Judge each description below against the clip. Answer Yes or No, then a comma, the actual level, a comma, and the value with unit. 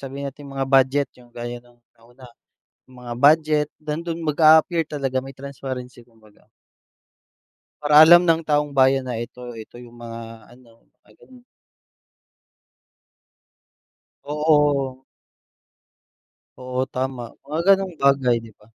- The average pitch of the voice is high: No, low, 135 Hz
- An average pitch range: Yes, average, 3.5 semitones